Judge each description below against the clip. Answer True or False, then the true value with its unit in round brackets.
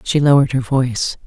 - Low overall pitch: True (130 Hz)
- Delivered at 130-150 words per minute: False (190 wpm)